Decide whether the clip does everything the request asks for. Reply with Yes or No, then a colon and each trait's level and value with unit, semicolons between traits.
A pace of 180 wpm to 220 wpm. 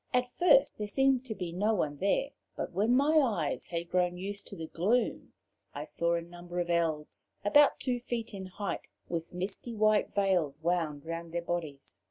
Yes: average, 190 wpm